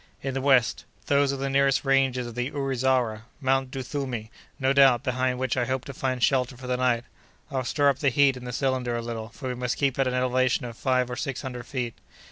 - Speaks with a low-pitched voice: Yes, low, 130 Hz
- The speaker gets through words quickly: Yes, fast, 225 wpm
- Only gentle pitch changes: Yes, narrow, 1.6 semitones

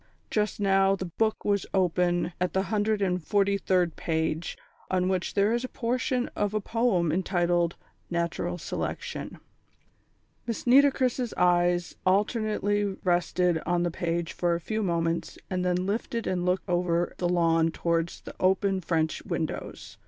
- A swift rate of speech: No, average, 150 wpm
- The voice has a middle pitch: Yes, medium, 180 Hz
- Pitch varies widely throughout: No, average, 3.0 semitones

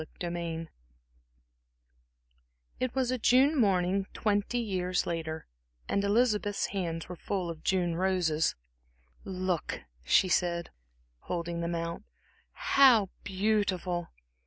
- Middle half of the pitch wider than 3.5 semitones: No, average, 3.2 semitones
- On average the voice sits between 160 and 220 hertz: Yes, medium, 185 Hz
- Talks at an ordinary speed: No, slow, 110 wpm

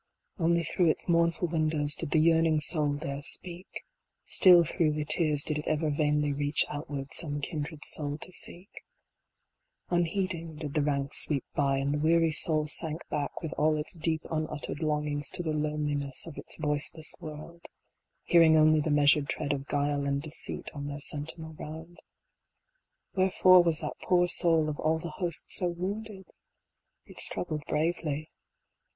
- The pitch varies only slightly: Yes, narrow, 2.3 semitones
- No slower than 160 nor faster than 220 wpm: Yes, average, 170 wpm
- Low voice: No, medium, 155 Hz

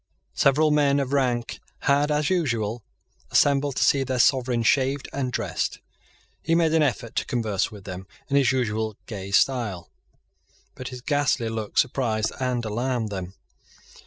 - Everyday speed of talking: Yes, average, 155 wpm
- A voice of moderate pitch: No, low, 125 Hz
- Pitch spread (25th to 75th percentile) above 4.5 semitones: No, average, 4.1 semitones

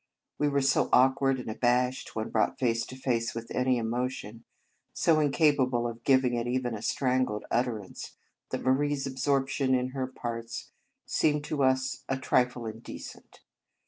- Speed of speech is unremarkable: Yes, average, 160 wpm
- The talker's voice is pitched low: Yes, low, 130 Hz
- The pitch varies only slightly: Yes, narrow, 2.2 semitones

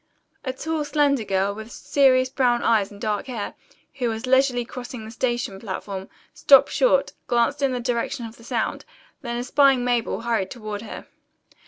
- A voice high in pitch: Yes, high, 240 Hz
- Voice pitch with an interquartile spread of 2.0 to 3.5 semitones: Yes, average, 3.0 semitones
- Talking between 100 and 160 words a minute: No, average, 170 wpm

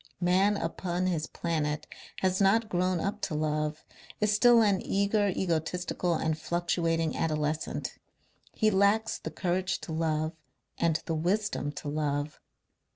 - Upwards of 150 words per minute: No, slow, 135 wpm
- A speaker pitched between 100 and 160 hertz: No, medium, 175 Hz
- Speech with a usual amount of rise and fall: Yes, average, 3.8 semitones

